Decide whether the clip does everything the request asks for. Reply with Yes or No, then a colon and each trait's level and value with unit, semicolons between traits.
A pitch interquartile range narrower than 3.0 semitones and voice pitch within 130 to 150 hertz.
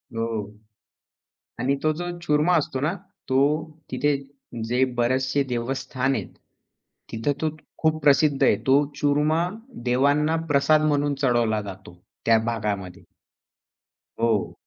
No: average, 4.1 semitones; low, 135 Hz